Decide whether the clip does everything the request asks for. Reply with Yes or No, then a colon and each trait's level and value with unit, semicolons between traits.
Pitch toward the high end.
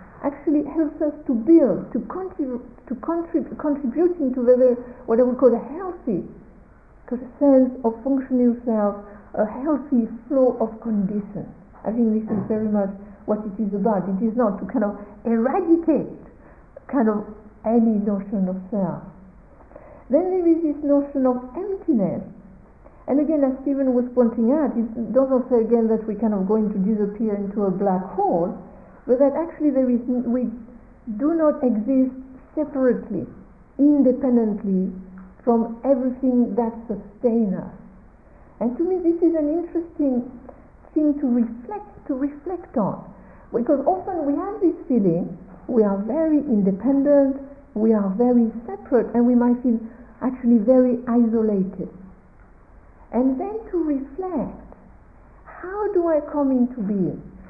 Yes: high, 245 Hz